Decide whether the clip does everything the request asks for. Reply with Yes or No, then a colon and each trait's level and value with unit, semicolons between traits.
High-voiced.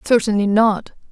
Yes: high, 215 Hz